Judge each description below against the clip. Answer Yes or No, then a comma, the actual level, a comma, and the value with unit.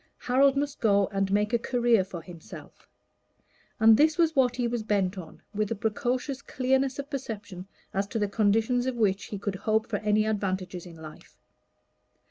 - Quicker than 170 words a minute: Yes, average, 180 wpm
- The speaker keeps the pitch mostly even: No, average, 4.1 semitones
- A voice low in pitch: No, high, 215 Hz